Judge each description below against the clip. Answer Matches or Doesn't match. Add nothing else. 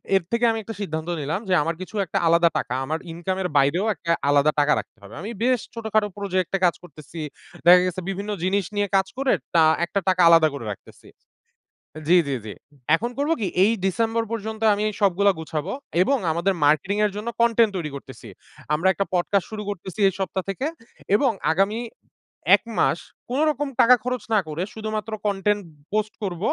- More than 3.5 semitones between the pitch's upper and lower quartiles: Matches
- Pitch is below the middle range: Doesn't match